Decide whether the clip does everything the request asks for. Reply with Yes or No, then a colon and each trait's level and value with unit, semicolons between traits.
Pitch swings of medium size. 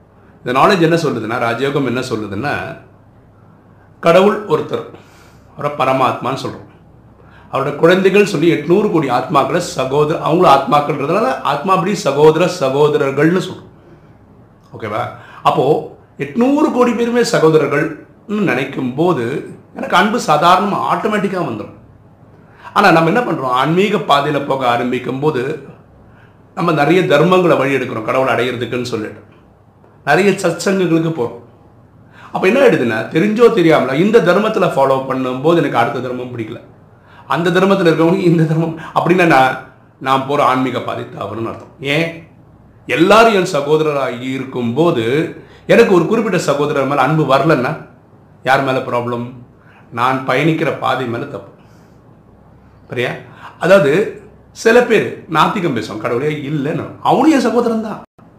No: wide, 5.8 semitones